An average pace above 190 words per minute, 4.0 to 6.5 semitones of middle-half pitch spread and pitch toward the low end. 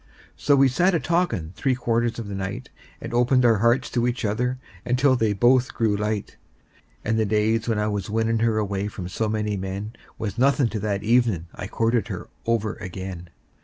No: average, 200 wpm; average, 3.0 semitones; low, 110 Hz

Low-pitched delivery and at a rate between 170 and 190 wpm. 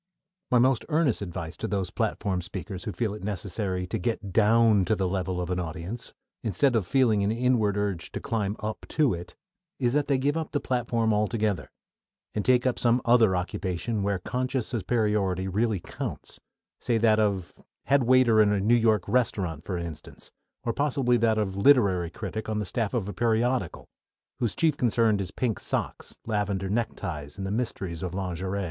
Yes: low, 105 Hz; average, 185 wpm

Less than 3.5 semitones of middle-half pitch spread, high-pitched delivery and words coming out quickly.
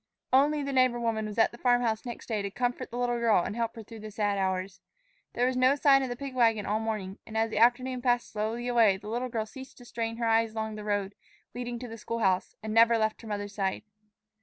Yes: narrow, 2.4 semitones; high, 230 Hz; fast, 260 wpm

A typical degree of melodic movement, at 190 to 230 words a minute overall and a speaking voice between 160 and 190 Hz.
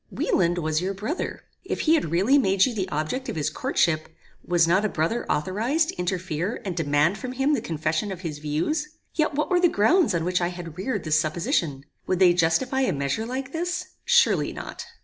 No: wide, 8.3 semitones; fast, 205 wpm; medium, 185 Hz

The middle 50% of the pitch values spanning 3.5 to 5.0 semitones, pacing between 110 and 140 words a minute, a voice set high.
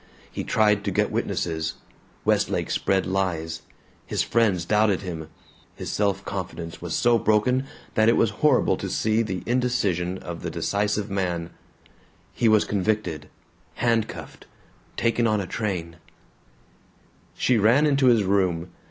No: average, 3.9 semitones; slow, 135 wpm; low, 100 Hz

